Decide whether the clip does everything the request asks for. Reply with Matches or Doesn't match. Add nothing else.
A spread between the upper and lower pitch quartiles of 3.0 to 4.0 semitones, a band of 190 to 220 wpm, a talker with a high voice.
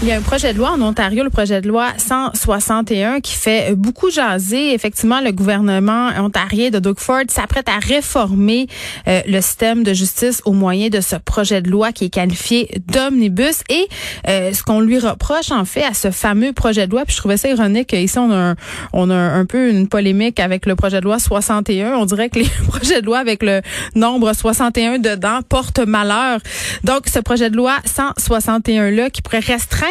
Matches